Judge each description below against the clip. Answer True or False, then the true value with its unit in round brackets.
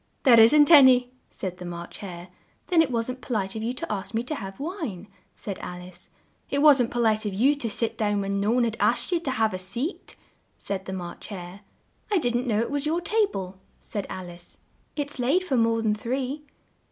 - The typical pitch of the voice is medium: False (230 Hz)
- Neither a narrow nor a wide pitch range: False (6.0 semitones)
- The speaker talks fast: True (225 wpm)